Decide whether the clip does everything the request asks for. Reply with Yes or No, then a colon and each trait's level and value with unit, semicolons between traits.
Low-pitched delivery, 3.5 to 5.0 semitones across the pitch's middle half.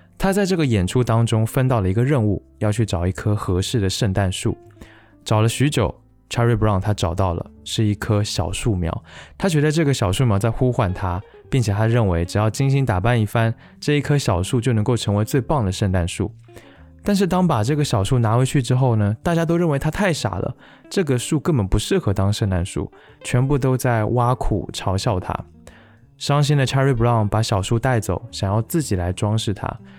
Yes: low, 115 Hz; average, 4.6 semitones